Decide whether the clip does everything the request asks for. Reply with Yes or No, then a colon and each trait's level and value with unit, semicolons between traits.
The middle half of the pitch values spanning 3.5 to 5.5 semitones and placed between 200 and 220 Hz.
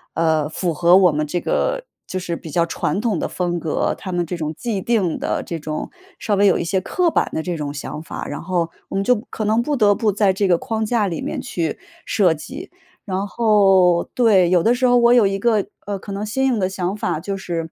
No: average, 4.2 semitones; high, 190 Hz